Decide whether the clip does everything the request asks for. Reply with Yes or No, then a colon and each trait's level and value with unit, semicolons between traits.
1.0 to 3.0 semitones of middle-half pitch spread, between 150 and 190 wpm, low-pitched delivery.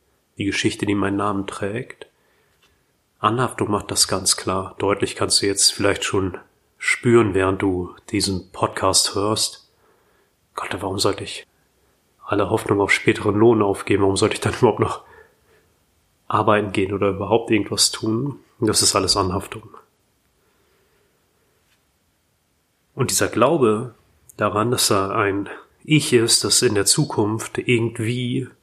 No: average, 2.7 semitones; average, 130 wpm; low, 105 Hz